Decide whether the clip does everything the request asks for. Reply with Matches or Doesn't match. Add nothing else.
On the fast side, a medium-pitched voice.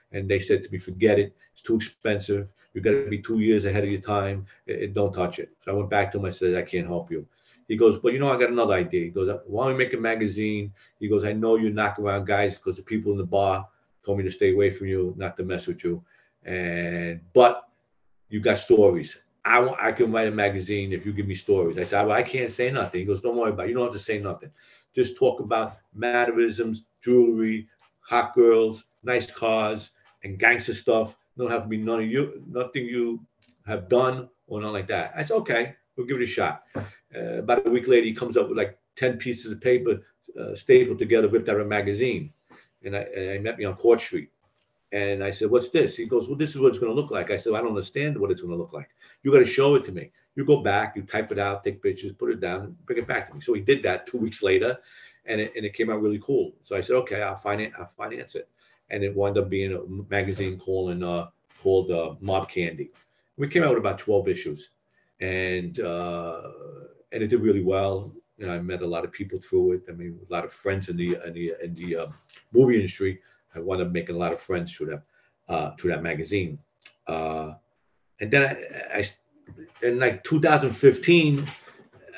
Doesn't match